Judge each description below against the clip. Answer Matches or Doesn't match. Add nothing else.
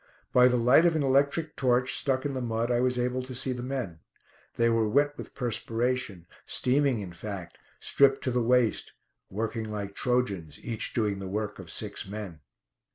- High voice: Doesn't match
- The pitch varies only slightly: Doesn't match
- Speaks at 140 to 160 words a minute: Doesn't match